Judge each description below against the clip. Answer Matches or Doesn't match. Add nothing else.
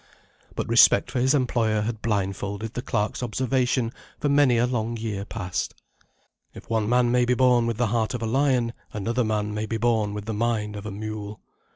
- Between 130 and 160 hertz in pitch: Doesn't match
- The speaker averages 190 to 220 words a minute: Matches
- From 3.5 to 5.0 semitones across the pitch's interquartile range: Doesn't match